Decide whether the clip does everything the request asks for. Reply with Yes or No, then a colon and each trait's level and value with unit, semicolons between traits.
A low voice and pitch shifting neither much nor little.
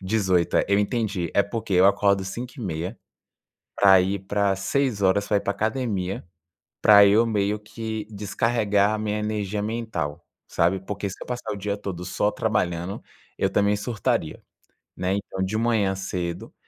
No: low, 100 Hz; narrow, 2.2 semitones